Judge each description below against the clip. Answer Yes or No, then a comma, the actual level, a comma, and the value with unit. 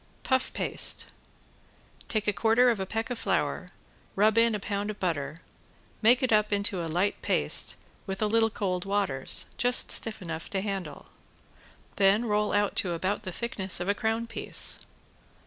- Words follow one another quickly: No, average, 170 wpm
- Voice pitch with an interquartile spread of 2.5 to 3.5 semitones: Yes, average, 2.8 semitones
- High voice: Yes, high, 205 Hz